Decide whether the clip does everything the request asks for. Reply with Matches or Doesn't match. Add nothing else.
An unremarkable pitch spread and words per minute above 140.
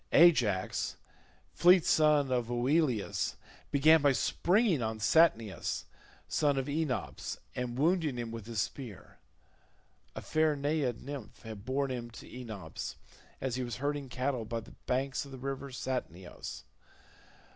Doesn't match